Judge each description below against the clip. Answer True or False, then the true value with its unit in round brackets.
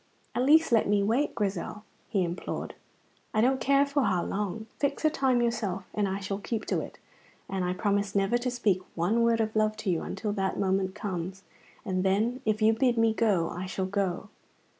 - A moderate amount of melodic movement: True (3.5 semitones)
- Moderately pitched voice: False (210 Hz)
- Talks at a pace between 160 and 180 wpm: False (205 wpm)